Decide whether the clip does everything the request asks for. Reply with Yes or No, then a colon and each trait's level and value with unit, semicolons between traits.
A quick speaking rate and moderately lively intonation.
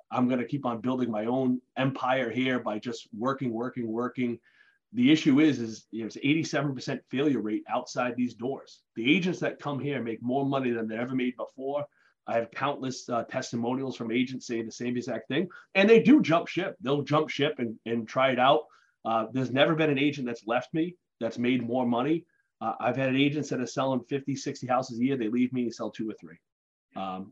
Yes: fast, 215 wpm; average, 3.2 semitones